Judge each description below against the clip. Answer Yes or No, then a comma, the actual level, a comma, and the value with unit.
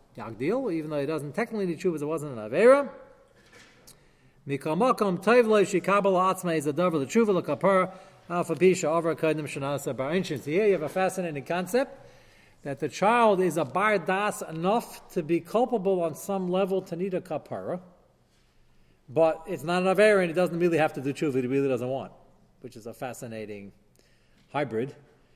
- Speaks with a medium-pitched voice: Yes, medium, 175 Hz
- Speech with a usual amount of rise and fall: Yes, average, 4.5 semitones